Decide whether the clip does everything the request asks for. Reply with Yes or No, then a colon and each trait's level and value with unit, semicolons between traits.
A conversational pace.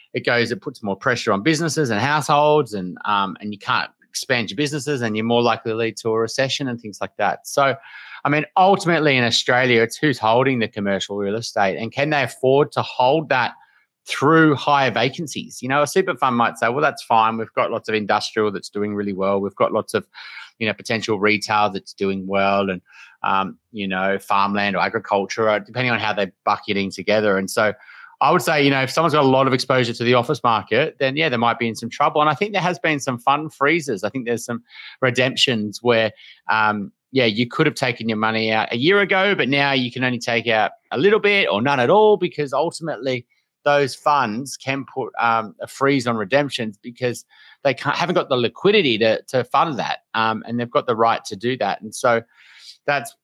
No: fast, 225 wpm